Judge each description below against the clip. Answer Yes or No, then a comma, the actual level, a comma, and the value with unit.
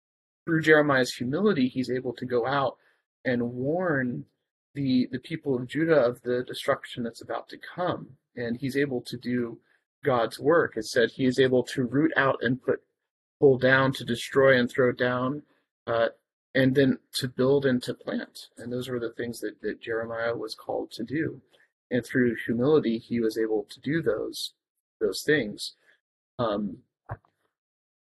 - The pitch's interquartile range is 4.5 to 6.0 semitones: No, narrow, 2.4 semitones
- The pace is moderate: Yes, average, 165 wpm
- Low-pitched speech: Yes, low, 125 Hz